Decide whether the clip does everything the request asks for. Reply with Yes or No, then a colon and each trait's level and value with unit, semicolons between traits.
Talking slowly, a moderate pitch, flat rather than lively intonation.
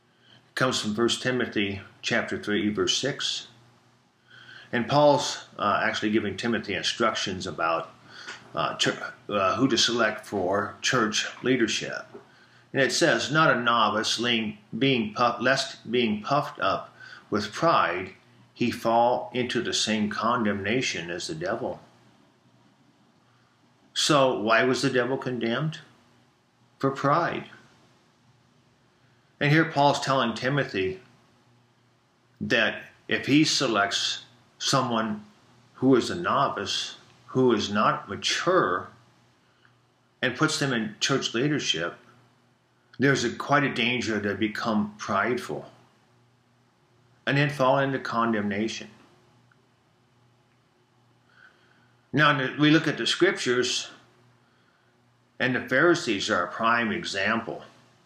No: slow, 110 wpm; low, 120 Hz; narrow, 2.3 semitones